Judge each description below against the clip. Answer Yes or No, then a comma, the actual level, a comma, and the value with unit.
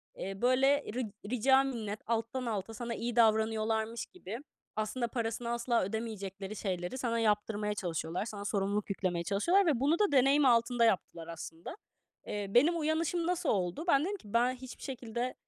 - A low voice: No, high, 230 Hz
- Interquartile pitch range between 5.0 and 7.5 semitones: No, average, 3.9 semitones